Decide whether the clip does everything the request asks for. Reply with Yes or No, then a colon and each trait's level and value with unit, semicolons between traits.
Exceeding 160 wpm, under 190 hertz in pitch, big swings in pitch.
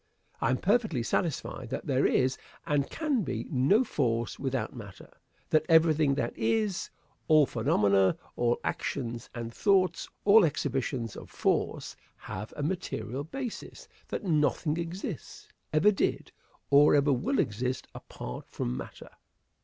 No: slow, 135 wpm; medium, 140 Hz; wide, 6.1 semitones